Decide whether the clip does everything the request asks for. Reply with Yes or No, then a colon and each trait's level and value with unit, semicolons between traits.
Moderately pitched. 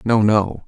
No: low, 105 Hz